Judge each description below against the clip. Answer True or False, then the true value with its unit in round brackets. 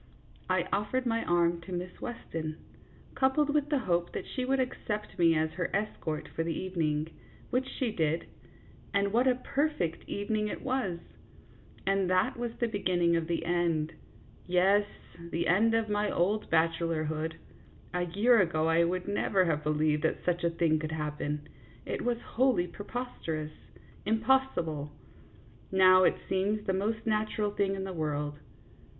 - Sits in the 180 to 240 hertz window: True (185 Hz)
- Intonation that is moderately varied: True (4.9 semitones)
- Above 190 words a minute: False (160 wpm)